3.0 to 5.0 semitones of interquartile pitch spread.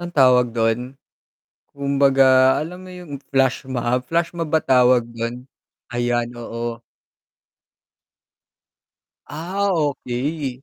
Yes: average, 3.7 semitones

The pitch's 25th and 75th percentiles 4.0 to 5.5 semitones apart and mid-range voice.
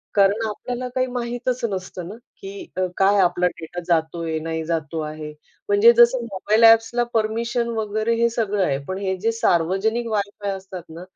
No: average, 4.6 semitones; high, 205 Hz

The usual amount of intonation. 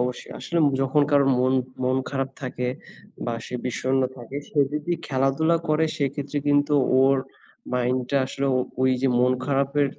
No: narrow, 2.0 semitones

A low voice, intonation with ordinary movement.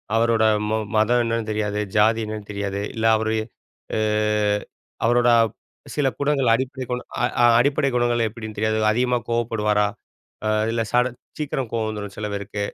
No: low, 115 Hz; narrow, 2.3 semitones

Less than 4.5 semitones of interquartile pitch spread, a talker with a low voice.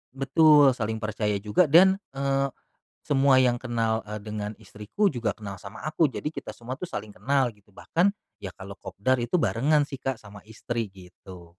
No: average, 4.8 semitones; low, 120 Hz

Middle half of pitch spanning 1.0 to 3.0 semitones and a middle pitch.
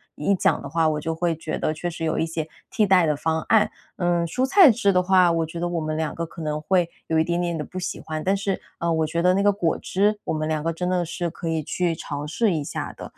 Yes: narrow, 2.4 semitones; medium, 170 Hz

